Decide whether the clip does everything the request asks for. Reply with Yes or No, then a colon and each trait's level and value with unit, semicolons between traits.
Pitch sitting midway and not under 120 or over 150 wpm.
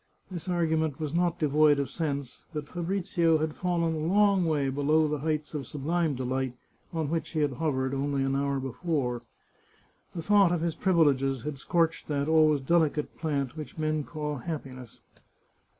No: medium, 155 Hz; average, 170 wpm